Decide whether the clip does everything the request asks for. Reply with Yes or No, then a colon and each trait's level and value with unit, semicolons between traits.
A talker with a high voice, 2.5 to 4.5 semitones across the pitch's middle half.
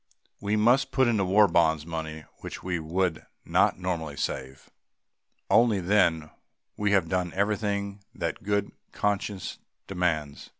No: very low, 95 Hz; average, 4.0 semitones